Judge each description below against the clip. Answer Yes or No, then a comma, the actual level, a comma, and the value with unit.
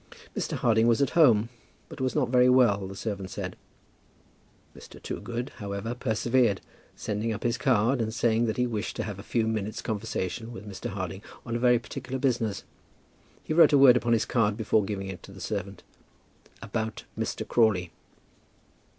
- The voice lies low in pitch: Yes, low, 110 Hz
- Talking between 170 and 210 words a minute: Yes, average, 175 wpm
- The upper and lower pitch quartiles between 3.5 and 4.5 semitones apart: No, average, 3.1 semitones